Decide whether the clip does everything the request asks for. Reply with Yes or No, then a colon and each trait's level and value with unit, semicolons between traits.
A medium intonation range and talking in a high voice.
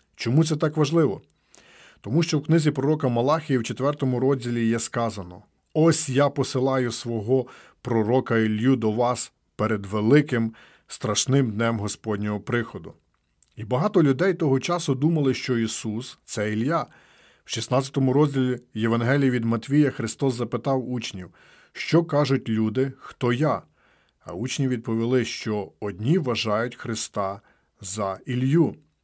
No: average, 3.6 semitones; low, 125 Hz